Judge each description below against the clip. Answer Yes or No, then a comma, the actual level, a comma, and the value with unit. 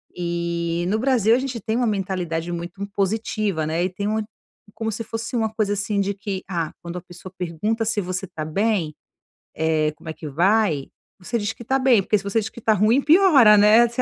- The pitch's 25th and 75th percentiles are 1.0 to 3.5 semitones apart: No, average, 4.3 semitones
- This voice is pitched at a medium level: No, high, 200 Hz